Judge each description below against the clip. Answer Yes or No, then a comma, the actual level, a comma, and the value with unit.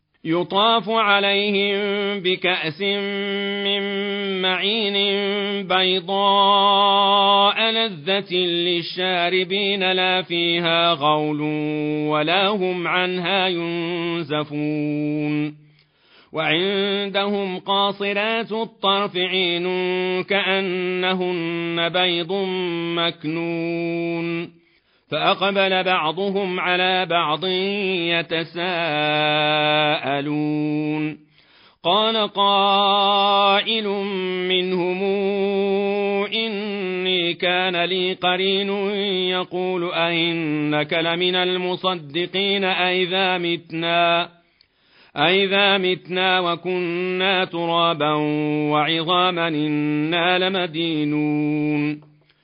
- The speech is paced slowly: Yes, slow, 55 wpm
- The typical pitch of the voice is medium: Yes, medium, 180 Hz